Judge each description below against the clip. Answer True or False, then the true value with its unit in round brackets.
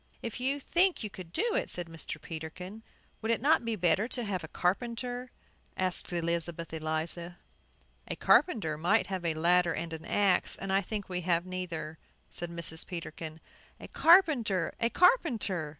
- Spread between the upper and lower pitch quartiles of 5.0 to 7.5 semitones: True (5.6 semitones)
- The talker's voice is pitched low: False (185 Hz)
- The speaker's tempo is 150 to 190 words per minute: True (165 wpm)